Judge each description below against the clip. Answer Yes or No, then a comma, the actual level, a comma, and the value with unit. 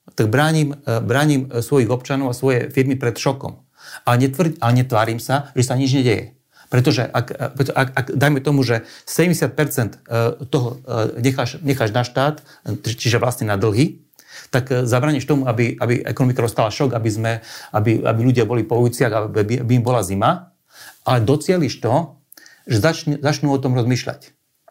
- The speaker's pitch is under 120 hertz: No, low, 130 Hz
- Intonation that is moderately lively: Yes, average, 3.1 semitones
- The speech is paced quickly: No, average, 155 wpm